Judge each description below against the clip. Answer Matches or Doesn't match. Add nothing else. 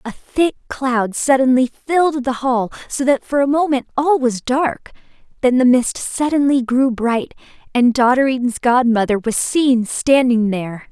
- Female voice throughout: Matches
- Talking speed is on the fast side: Doesn't match